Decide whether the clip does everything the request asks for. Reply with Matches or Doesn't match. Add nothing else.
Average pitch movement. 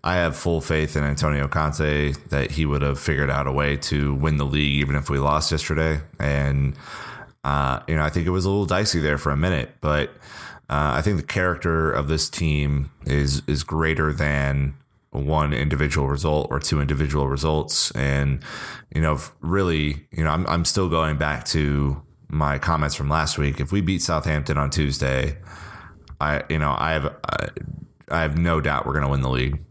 Doesn't match